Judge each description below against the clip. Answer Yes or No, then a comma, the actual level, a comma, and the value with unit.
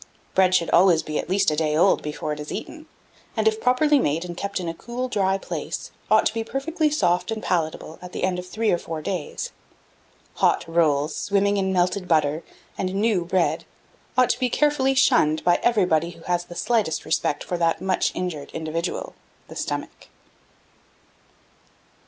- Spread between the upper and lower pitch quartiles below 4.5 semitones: No, average, 5.2 semitones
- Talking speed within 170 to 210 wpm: Yes, average, 180 wpm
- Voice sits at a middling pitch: Yes, medium, 180 Hz